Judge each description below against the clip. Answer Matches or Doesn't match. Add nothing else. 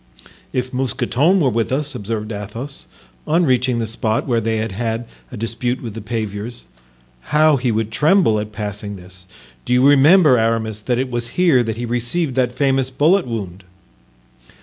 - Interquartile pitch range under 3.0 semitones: Doesn't match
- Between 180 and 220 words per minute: Doesn't match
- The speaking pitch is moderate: Doesn't match